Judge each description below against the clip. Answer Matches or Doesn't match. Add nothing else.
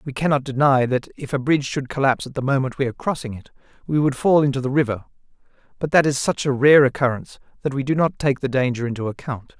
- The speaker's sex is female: Doesn't match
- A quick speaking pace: Matches